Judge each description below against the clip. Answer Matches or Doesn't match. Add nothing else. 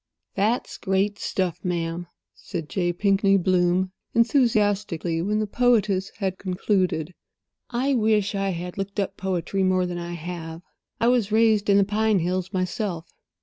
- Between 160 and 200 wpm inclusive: Doesn't match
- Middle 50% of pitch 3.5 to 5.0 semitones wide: Doesn't match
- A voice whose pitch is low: Doesn't match